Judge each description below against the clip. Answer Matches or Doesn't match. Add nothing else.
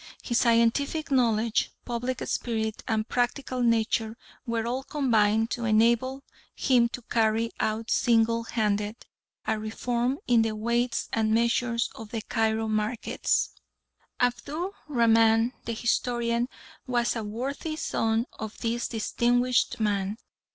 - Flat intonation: Matches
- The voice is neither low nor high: Doesn't match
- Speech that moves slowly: Matches